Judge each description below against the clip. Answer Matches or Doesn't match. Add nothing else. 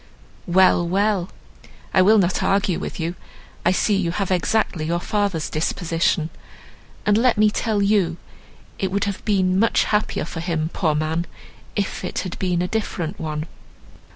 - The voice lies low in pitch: Doesn't match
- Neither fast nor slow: Matches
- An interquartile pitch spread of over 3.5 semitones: Doesn't match